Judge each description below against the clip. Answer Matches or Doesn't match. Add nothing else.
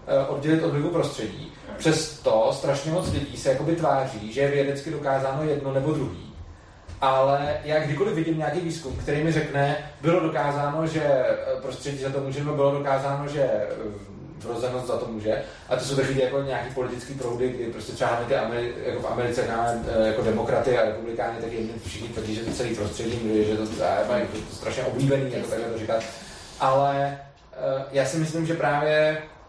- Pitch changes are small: Doesn't match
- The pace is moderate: Doesn't match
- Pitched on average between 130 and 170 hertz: Matches